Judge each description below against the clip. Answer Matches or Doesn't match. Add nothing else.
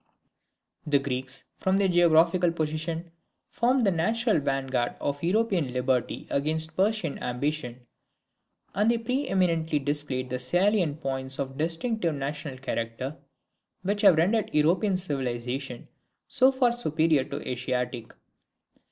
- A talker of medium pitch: Matches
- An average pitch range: Doesn't match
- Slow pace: Matches